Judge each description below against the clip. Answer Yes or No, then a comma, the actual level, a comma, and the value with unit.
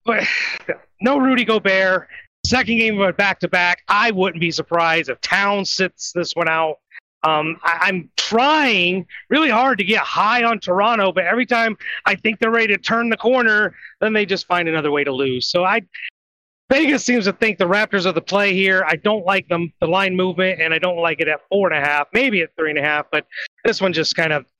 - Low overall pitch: No, high, 190 Hz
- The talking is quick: Yes, fast, 225 wpm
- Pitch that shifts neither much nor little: Yes, average, 4.7 semitones